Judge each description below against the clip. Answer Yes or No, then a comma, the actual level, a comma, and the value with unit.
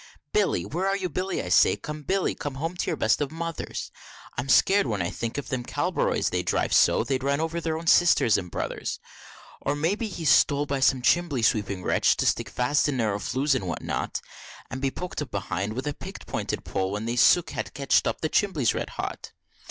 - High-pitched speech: No, medium, 140 Hz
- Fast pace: Yes, fast, 225 wpm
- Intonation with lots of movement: Yes, wide, 6.2 semitones